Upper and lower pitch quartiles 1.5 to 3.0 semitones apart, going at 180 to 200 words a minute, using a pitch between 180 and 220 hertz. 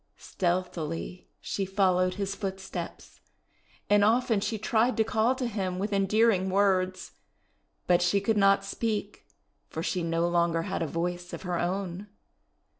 No: narrow, 2.6 semitones; average, 145 wpm; high, 190 Hz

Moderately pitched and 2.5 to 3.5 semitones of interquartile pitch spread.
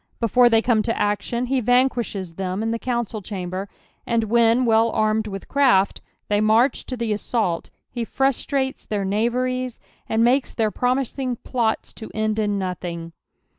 No: high, 225 Hz; average, 3.1 semitones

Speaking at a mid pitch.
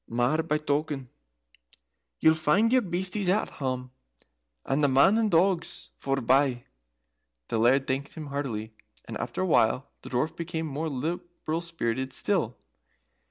Yes: medium, 150 Hz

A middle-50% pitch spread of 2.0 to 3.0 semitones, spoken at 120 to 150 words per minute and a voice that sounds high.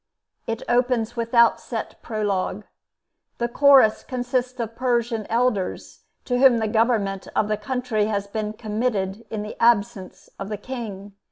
Yes: average, 2.7 semitones; average, 145 wpm; high, 225 Hz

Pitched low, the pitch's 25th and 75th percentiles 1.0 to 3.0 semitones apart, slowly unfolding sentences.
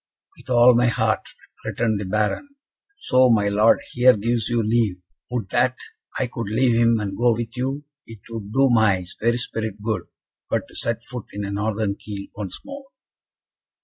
No: low, 115 Hz; average, 2.7 semitones; average, 180 wpm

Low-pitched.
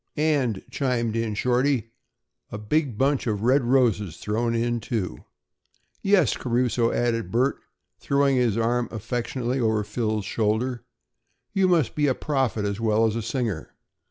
Yes: low, 120 Hz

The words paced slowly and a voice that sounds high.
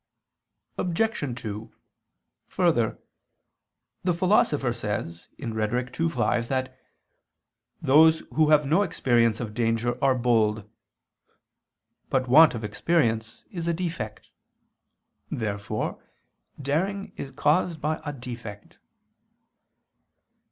No: slow, 95 wpm; low, 130 Hz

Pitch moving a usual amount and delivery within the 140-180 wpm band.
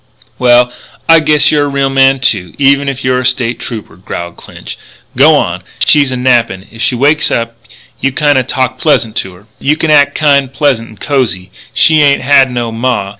No: average, 3.4 semitones; average, 190 wpm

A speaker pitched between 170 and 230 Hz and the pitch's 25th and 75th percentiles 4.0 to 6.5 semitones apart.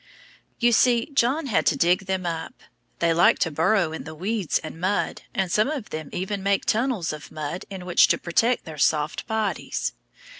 Yes: medium, 185 Hz; average, 5.1 semitones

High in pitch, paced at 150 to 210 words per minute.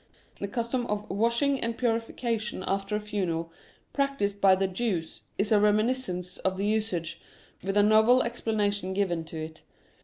Yes: high, 210 Hz; average, 160 wpm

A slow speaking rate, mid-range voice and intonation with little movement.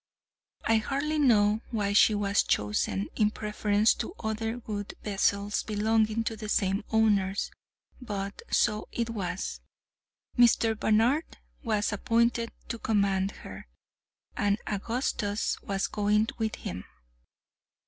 No: slow, 115 wpm; high, 215 Hz; narrow, 1.8 semitones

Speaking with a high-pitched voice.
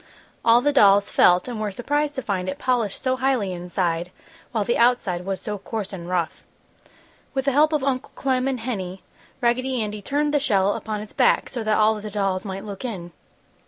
Yes: high, 215 Hz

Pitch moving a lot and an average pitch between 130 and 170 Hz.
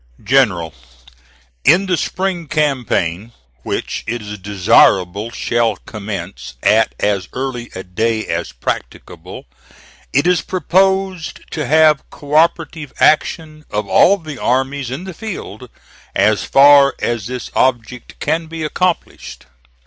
Yes: wide, 7.0 semitones; low, 135 Hz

